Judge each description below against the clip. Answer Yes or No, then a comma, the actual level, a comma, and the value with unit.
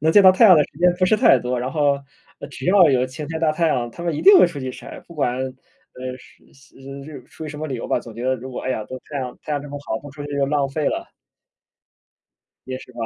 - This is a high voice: No, medium, 140 Hz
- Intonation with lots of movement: No, average, 3.6 semitones